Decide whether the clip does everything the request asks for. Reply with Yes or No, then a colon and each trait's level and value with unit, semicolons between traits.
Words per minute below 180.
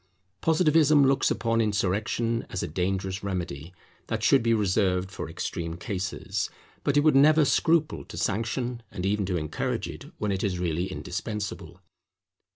Yes: average, 155 wpm